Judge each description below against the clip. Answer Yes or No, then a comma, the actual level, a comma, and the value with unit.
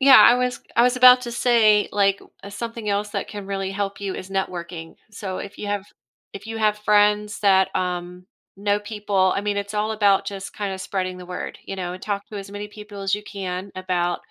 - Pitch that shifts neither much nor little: No, narrow, 1.7 semitones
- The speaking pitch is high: Yes, high, 200 Hz